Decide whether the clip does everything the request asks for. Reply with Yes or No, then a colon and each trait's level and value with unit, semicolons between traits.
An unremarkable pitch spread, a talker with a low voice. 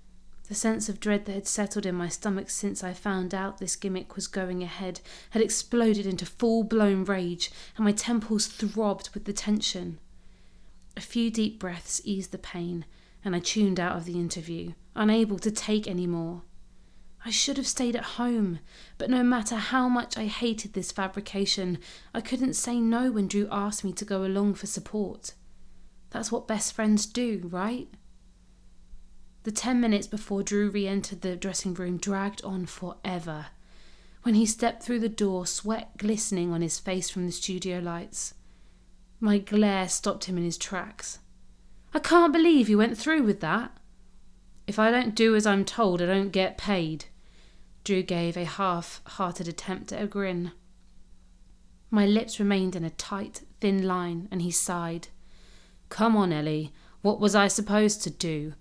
No: average, 3.5 semitones; high, 195 Hz